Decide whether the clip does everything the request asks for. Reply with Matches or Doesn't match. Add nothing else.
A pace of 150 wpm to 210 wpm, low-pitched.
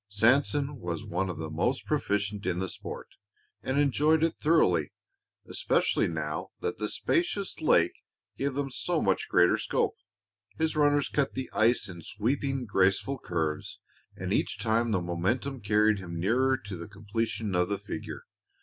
Matches